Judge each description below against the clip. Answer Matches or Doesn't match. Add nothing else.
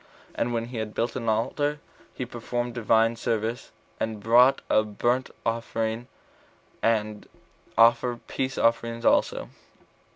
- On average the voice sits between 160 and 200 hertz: Doesn't match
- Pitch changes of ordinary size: Doesn't match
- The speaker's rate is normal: Doesn't match